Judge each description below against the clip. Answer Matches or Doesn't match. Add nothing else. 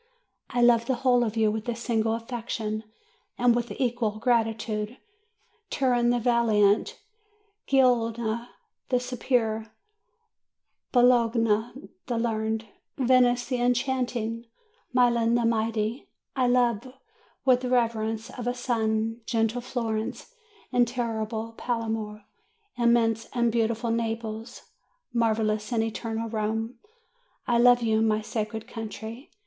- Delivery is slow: Matches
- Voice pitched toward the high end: Matches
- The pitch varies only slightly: Matches